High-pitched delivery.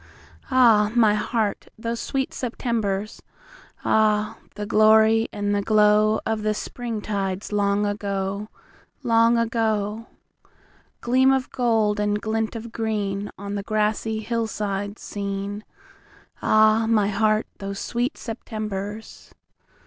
Yes: high, 215 Hz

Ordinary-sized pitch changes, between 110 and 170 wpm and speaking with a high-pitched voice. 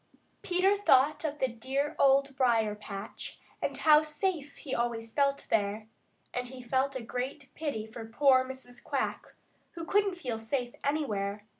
Yes: average, 4.4 semitones; average, 155 wpm; very high, 260 Hz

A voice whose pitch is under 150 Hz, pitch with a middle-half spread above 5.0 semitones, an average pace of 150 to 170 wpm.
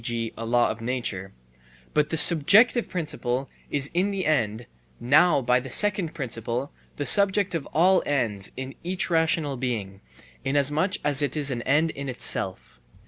Yes: medium, 140 Hz; wide, 5.4 semitones; average, 160 wpm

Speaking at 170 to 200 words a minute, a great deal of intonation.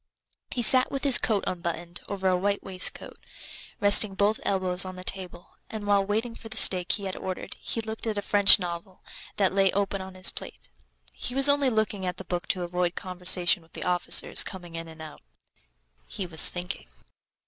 No: average, 195 wpm; narrow, 2.4 semitones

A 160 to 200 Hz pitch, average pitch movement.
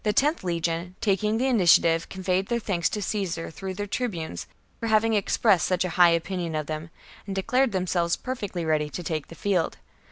Yes: medium, 185 Hz; average, 3.8 semitones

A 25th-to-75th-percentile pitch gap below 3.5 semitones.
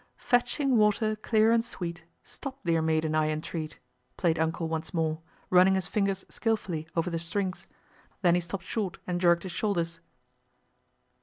No: average, 4.4 semitones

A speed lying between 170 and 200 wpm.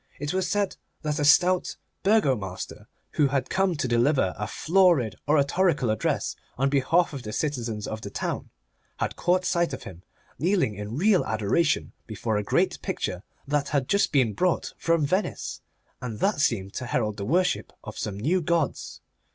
Yes: average, 175 wpm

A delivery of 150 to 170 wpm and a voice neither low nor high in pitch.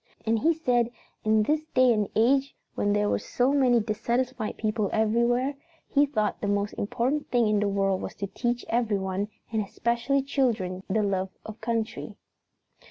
No: average, 165 wpm; high, 225 Hz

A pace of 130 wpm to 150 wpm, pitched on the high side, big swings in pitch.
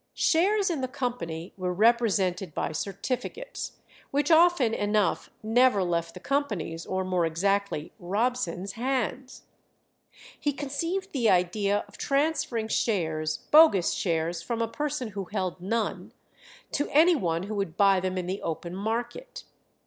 Yes: average, 140 wpm; high, 210 Hz; wide, 6.5 semitones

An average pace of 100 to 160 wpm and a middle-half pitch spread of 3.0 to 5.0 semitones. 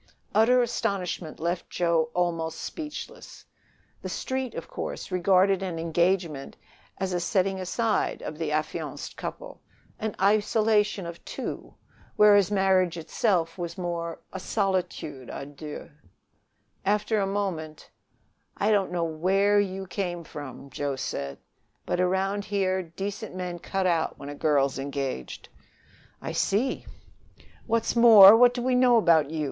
Yes: average, 140 wpm; average, 3.8 semitones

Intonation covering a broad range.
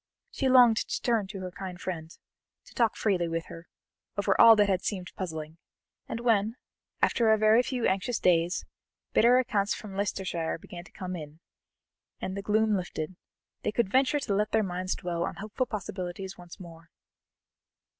No: average, 3.7 semitones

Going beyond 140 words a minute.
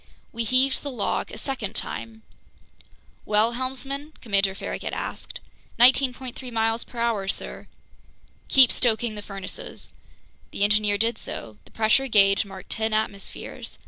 No: slow, 135 wpm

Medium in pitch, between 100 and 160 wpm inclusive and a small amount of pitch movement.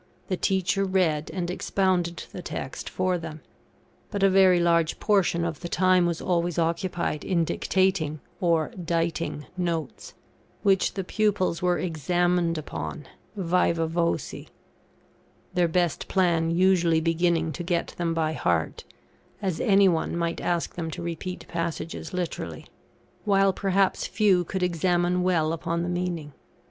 Yes: medium, 175 Hz; average, 140 wpm; narrow, 1.9 semitones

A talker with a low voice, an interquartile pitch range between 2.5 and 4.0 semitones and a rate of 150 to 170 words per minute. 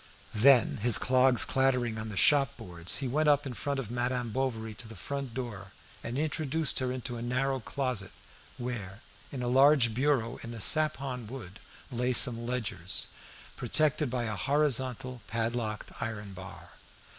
Yes: low, 125 Hz; average, 3.1 semitones; average, 155 wpm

